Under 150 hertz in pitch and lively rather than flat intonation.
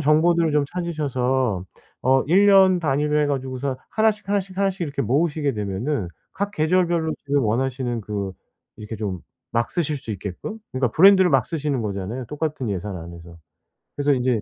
Yes: medium, 140 Hz; wide, 6.5 semitones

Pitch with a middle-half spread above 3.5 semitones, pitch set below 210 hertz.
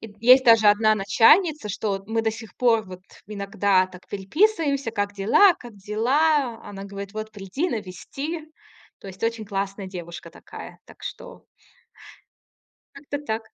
No: average, 4.5 semitones; high, 220 Hz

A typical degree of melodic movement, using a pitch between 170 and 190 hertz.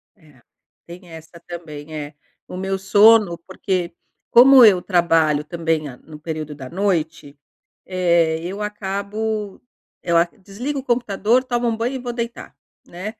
Yes: average, 4.9 semitones; medium, 185 Hz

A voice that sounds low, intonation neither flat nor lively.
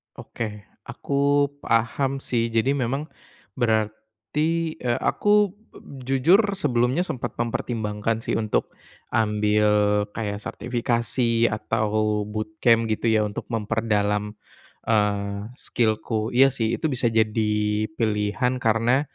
Yes: low, 115 Hz; average, 3.2 semitones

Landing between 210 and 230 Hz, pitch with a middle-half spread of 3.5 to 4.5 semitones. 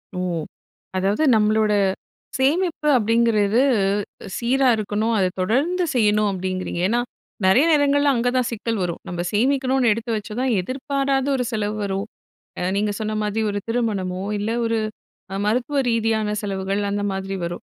Yes: high, 220 Hz; average, 3.9 semitones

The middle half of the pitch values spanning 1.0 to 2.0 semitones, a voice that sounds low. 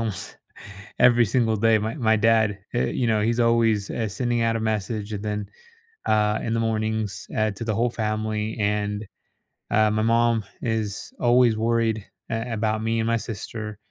Yes: narrow, 1.3 semitones; low, 110 Hz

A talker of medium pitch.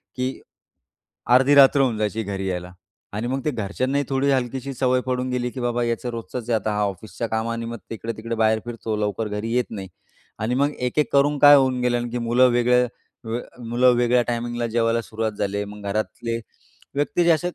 No: low, 120 Hz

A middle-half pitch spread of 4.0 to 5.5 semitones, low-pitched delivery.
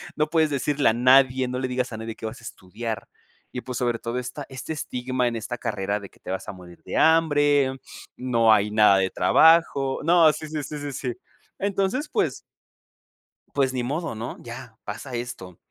Yes: average, 4.4 semitones; low, 125 Hz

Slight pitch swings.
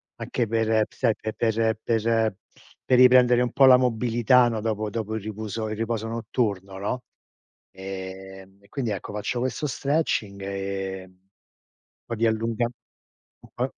No: average, 3.3 semitones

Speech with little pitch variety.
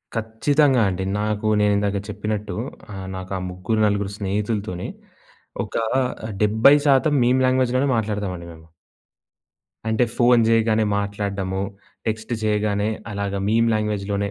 Yes: narrow, 2.1 semitones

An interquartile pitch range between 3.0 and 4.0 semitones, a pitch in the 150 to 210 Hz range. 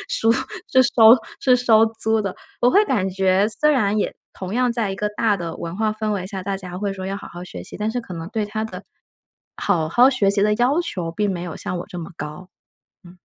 Yes: average, 3.5 semitones; high, 205 Hz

